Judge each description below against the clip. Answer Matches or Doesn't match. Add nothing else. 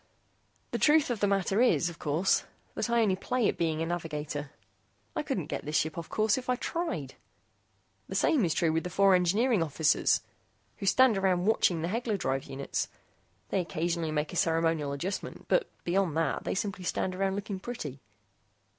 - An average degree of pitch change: Matches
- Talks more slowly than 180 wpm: Doesn't match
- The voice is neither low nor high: Matches